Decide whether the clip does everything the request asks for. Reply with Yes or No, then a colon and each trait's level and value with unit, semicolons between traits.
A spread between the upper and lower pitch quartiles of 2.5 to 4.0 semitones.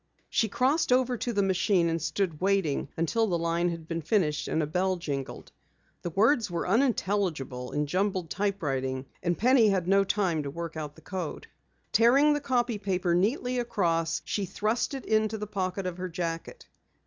No: average, 4.6 semitones